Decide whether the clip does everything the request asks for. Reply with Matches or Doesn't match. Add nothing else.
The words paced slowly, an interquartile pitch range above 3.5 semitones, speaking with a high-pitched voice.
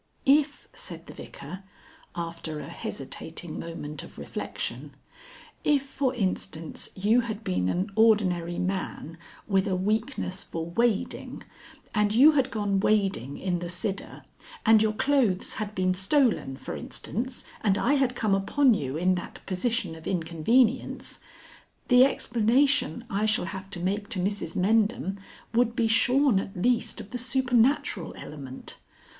Doesn't match